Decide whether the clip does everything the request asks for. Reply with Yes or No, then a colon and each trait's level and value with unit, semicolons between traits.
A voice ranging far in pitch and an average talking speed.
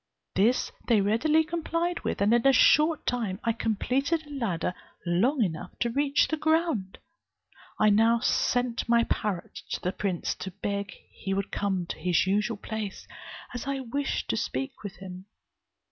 Yes: wide, 5.8 semitones; average, 165 wpm